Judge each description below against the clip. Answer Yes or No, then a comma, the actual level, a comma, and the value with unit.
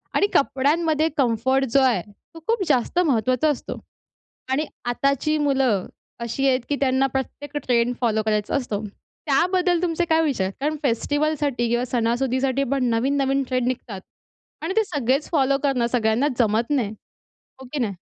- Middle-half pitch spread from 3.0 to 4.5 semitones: Yes, average, 3.5 semitones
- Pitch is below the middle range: No, very high, 265 Hz